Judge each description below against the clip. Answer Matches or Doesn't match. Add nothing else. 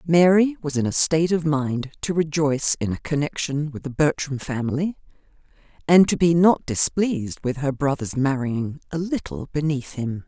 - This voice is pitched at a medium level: Matches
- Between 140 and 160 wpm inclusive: Doesn't match